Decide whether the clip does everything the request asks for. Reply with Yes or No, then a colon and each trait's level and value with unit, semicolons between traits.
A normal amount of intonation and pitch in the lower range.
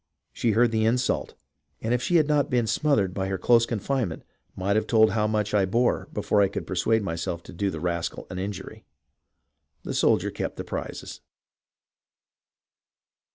Yes: average, 3.7 semitones; low, 110 Hz